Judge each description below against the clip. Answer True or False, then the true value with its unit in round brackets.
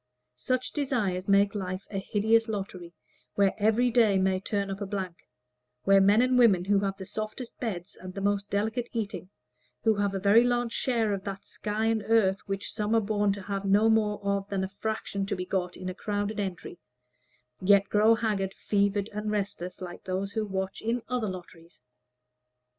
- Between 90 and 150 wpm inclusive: False (190 wpm)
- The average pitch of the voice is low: False (200 Hz)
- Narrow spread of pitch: True (2.2 semitones)